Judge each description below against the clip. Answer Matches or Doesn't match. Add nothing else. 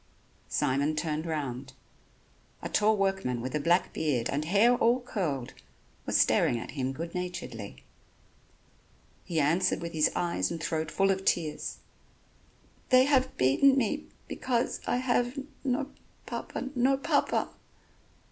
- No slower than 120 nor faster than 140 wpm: Matches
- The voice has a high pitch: Doesn't match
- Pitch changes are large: Matches